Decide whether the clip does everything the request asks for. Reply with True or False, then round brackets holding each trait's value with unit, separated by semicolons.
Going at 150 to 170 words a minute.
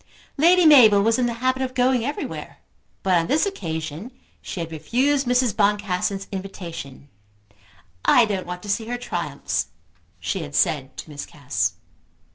True (155 wpm)